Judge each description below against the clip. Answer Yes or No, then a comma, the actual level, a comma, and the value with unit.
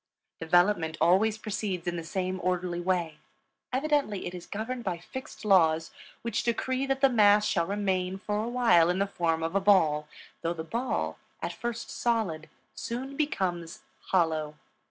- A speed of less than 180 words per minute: Yes, average, 160 wpm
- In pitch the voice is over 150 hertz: Yes, high, 190 Hz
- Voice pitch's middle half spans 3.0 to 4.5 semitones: No, average, 4.9 semitones